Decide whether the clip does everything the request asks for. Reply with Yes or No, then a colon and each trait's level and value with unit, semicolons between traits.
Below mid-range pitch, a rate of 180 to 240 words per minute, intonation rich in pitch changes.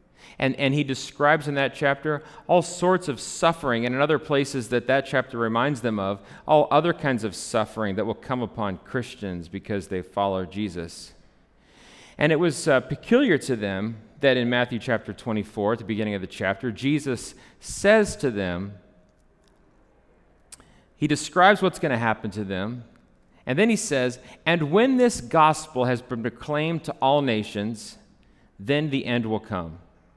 No: low, 125 Hz; average, 165 wpm; wide, 5.7 semitones